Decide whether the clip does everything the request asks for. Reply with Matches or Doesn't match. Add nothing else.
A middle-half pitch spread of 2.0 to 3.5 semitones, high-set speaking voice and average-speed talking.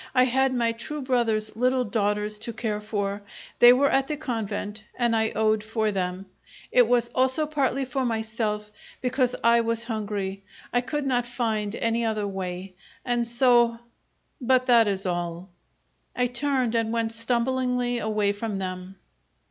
Matches